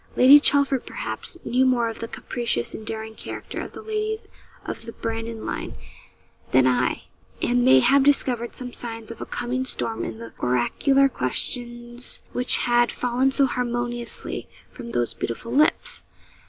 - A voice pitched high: Yes, high, 240 Hz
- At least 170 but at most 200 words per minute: No, average, 155 wpm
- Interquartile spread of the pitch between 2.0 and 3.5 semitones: Yes, average, 2.9 semitones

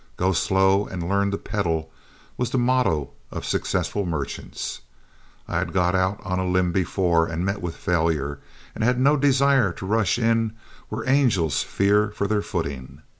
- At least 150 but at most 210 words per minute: Yes, average, 170 wpm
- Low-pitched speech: Yes, very low, 95 Hz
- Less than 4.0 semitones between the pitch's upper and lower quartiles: No, average, 4.5 semitones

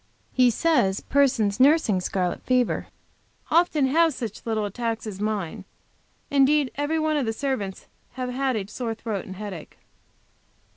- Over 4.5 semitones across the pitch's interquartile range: Yes, average, 5.2 semitones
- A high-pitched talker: Yes, high, 245 Hz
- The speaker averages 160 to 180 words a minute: No, average, 145 wpm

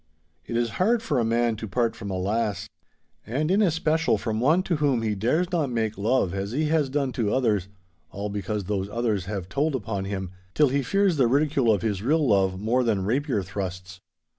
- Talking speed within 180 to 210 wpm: Yes, fast, 205 wpm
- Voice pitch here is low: Yes, low, 115 Hz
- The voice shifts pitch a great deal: Yes, wide, 6.0 semitones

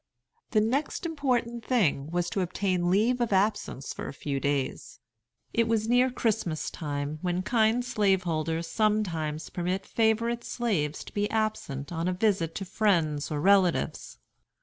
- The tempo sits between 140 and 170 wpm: Yes, average, 150 wpm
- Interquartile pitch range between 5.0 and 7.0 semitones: Yes, wide, 5.6 semitones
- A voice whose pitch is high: Yes, high, 195 Hz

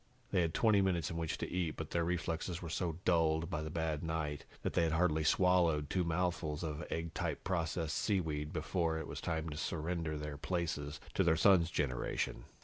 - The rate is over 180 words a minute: Yes, average, 200 wpm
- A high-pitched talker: No, very low, 80 Hz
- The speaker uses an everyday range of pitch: No, narrow, 2.0 semitones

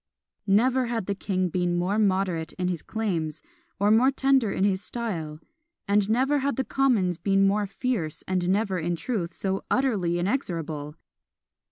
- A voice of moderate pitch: No, high, 195 Hz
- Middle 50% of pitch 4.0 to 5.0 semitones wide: Yes, average, 4.6 semitones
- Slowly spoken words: No, average, 160 wpm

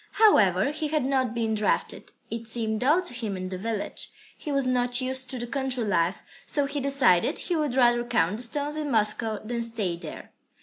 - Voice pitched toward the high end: Yes, high, 240 Hz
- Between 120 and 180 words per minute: No, fast, 205 wpm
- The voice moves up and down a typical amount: Yes, average, 4.1 semitones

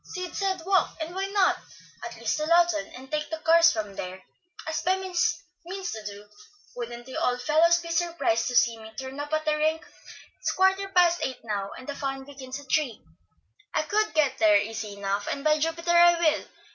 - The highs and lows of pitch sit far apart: Yes, wide, 5.8 semitones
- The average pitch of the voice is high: Yes, very high, 305 Hz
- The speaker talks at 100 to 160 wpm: No, fast, 205 wpm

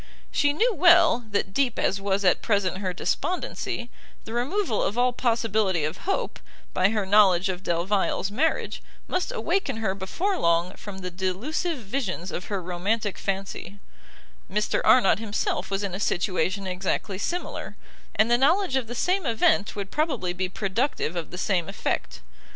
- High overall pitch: Yes, high, 205 Hz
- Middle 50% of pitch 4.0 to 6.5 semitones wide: Yes, average, 5.1 semitones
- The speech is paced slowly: No, average, 160 wpm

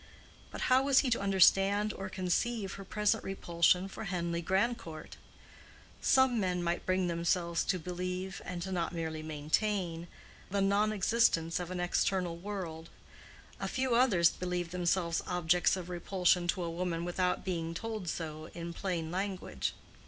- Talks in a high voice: No, medium, 180 Hz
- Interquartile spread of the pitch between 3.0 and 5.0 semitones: No, narrow, 2.5 semitones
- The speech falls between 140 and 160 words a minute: Yes, average, 145 wpm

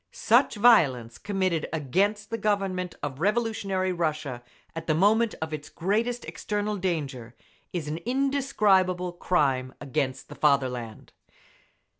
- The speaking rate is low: Yes, slow, 120 wpm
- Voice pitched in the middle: Yes, medium, 180 Hz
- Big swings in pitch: Yes, wide, 6.2 semitones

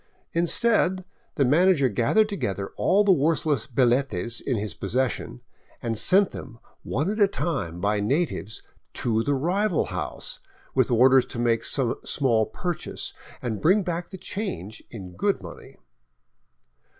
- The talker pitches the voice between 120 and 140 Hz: Yes, low, 135 Hz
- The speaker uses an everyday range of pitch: No, wide, 7.9 semitones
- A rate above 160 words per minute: No, average, 140 wpm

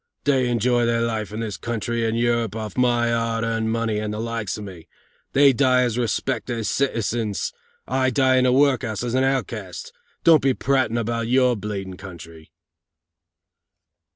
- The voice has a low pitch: Yes, low, 115 Hz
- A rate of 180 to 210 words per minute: No, average, 160 wpm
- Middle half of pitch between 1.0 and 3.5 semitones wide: Yes, average, 2.8 semitones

